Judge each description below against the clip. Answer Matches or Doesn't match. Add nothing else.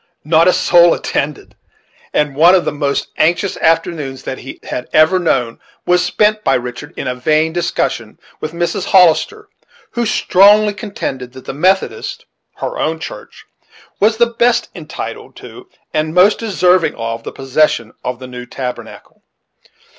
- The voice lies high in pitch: Doesn't match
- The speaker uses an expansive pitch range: Matches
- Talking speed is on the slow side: Doesn't match